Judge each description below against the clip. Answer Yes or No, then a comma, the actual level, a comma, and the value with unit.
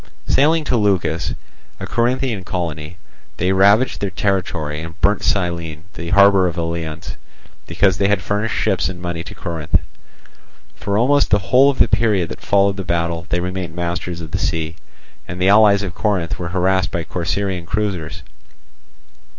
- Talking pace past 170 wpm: No, average, 165 wpm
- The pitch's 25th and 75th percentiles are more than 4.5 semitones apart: No, average, 3.2 semitones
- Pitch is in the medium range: No, very low, 90 Hz